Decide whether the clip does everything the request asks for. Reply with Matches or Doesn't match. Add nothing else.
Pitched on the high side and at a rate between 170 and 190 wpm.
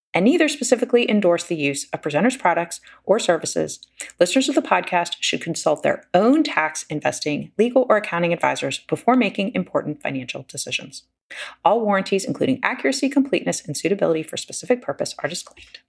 Doesn't match